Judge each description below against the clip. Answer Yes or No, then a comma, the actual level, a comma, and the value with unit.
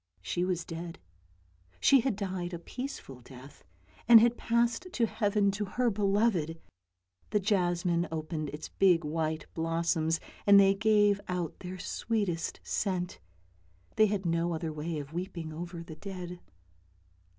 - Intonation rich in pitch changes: No, average, 3.8 semitones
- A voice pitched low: No, medium, 175 Hz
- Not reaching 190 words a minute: Yes, average, 145 wpm